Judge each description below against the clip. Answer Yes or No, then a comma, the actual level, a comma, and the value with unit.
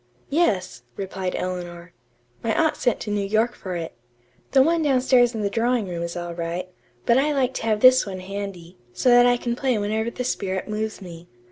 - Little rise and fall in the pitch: No, average, 5.1 semitones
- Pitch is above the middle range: Yes, high, 210 Hz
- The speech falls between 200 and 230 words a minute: Yes, fast, 205 wpm